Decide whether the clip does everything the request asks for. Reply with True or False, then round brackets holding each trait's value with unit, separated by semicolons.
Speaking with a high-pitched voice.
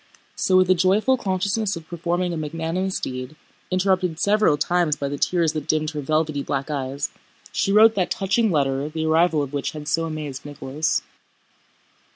False (160 Hz)